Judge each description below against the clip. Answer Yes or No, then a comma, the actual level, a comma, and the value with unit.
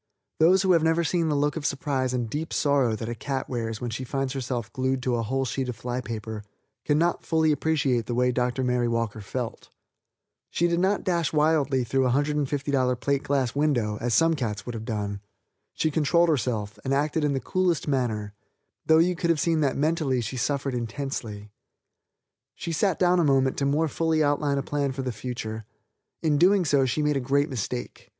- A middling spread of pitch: Yes, average, 4.1 semitones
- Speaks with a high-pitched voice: No, low, 135 Hz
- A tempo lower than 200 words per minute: No, fast, 205 wpm